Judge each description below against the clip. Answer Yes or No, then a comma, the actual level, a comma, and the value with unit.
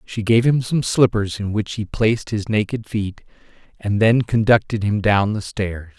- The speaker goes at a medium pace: Yes, average, 190 wpm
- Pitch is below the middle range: Yes, low, 105 Hz